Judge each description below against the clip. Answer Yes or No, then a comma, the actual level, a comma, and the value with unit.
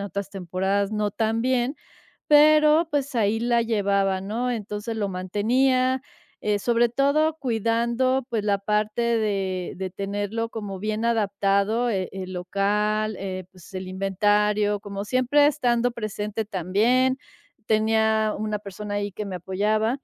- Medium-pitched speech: No, high, 215 Hz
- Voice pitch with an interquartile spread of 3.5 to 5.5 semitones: No, average, 3.0 semitones